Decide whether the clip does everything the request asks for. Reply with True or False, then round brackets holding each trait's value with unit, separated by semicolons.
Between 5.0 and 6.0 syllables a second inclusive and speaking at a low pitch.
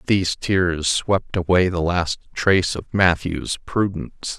False (4.0 syllables/s; 90 Hz)